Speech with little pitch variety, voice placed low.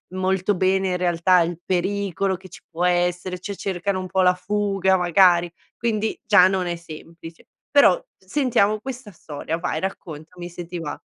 No: narrow, 2.0 semitones; medium, 185 Hz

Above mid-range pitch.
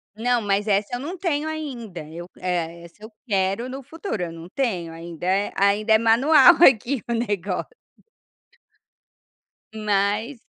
Yes: high, 210 Hz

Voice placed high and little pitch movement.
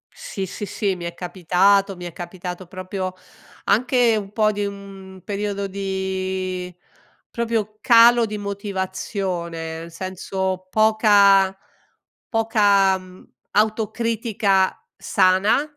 Yes: high, 195 Hz; narrow, 2.3 semitones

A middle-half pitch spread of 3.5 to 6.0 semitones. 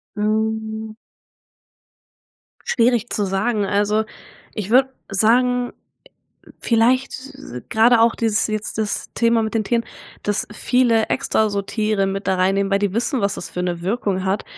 No: average, 2.7 semitones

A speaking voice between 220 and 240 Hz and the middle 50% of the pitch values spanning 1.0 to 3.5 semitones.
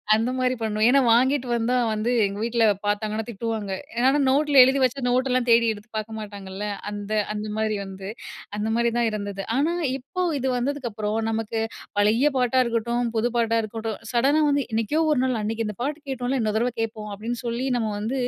Yes: high, 230 Hz; average, 3.0 semitones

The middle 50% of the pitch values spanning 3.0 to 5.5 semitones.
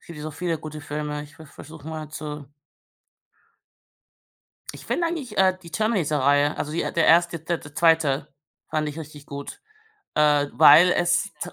No: narrow, 2.5 semitones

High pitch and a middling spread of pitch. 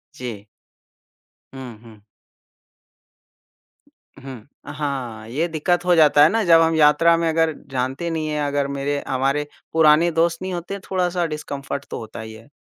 No: medium, 150 Hz; average, 3.8 semitones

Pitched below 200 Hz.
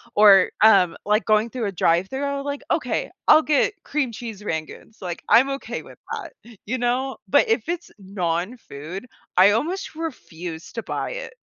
No: high, 220 Hz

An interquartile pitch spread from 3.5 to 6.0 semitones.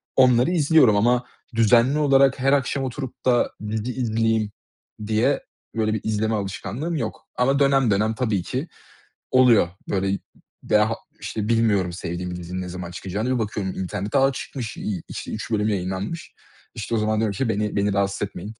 Yes: average, 4.2 semitones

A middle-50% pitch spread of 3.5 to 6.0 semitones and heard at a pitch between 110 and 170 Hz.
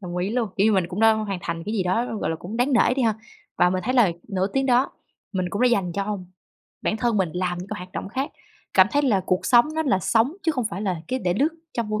No: average, 4.7 semitones; high, 210 Hz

